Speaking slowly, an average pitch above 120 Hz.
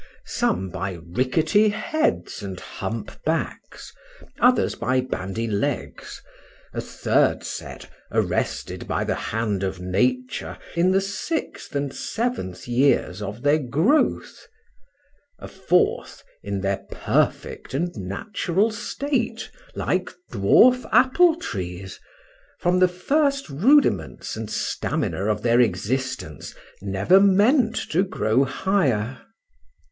Yes: slow, 105 wpm; medium, 140 Hz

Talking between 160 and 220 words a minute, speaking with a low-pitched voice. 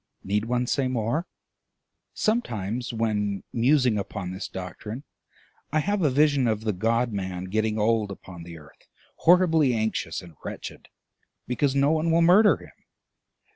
No: average, 145 wpm; low, 115 Hz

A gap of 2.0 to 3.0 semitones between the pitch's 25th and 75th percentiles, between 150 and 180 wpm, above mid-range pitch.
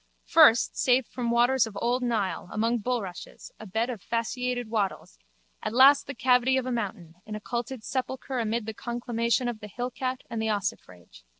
Yes: narrow, 2.5 semitones; average, 175 wpm; high, 235 Hz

